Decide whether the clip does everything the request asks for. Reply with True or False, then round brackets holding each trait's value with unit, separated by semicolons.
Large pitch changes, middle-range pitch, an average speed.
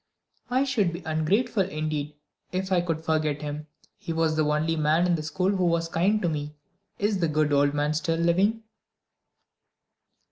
False (3.3 semitones; 165 Hz; 175 wpm)